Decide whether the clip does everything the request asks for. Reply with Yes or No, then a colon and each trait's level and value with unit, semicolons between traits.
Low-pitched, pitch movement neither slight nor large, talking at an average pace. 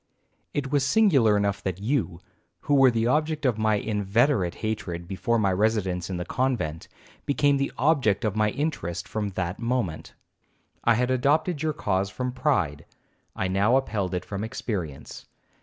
No: low, 110 Hz; wide, 5.8 semitones; average, 160 wpm